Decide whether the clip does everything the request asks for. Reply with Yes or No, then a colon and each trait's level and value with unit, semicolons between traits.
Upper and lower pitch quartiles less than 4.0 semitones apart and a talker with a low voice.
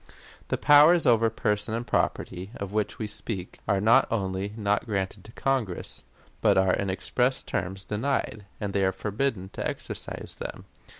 Yes: average, 3.2 semitones; low, 105 Hz